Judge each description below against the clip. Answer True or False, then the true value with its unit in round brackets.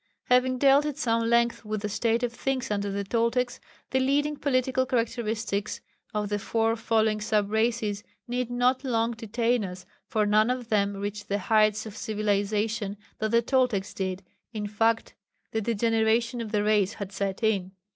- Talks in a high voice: True (225 Hz)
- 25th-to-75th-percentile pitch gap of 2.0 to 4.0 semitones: True (2.6 semitones)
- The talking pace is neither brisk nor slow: True (170 wpm)